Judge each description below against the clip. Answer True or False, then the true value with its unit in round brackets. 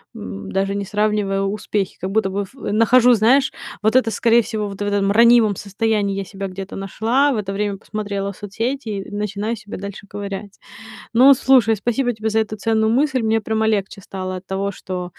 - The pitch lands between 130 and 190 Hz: False (210 Hz)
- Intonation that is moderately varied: False (2.3 semitones)